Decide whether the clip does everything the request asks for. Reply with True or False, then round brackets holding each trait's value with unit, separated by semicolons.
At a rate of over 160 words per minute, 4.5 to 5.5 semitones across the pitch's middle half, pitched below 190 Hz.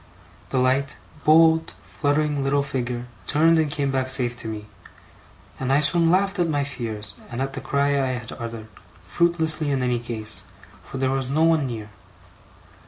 False (170 wpm; 3.8 semitones; 135 Hz)